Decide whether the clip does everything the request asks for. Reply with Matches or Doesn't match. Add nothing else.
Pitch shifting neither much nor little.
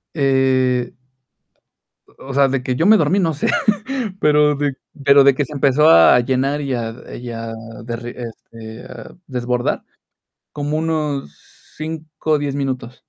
Matches